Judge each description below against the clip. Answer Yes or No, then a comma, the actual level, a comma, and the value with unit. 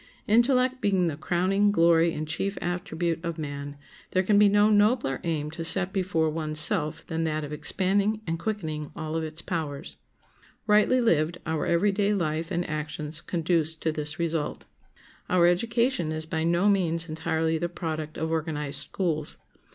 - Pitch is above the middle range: No, medium, 165 Hz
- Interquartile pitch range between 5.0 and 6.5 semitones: No, average, 3.5 semitones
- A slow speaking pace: No, average, 165 wpm